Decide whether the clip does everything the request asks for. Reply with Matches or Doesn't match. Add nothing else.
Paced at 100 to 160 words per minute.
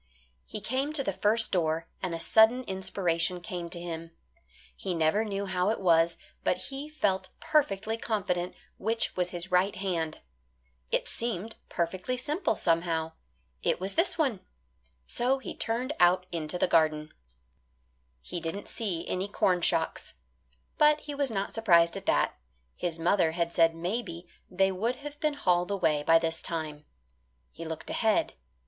Matches